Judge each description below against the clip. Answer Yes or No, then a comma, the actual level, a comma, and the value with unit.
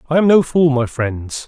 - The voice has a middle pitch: Yes, medium, 145 Hz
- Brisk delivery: Yes, fast, 245 wpm